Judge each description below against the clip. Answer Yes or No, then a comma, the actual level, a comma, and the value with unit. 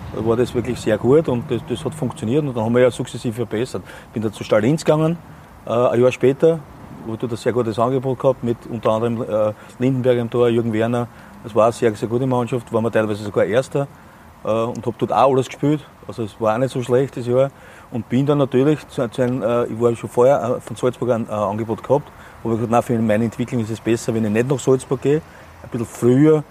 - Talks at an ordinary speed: No, fast, 220 wpm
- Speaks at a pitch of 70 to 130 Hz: Yes, low, 120 Hz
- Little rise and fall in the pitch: Yes, narrow, 2.3 semitones